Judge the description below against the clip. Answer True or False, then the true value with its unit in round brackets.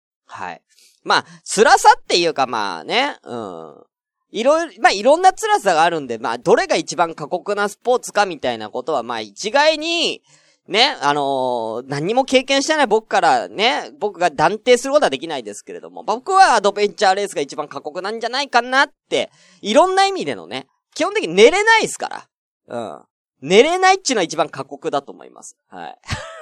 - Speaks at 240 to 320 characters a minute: False (380 characters per minute)